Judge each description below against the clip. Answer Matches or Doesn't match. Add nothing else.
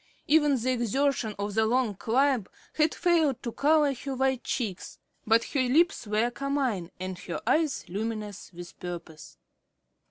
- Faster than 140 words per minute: Matches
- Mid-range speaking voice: Doesn't match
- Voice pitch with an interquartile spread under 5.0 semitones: Doesn't match